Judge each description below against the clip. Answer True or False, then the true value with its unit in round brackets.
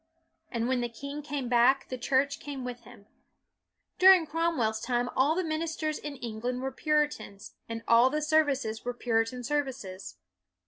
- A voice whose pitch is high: True (260 Hz)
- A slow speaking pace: False (165 wpm)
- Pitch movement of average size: True (4.0 semitones)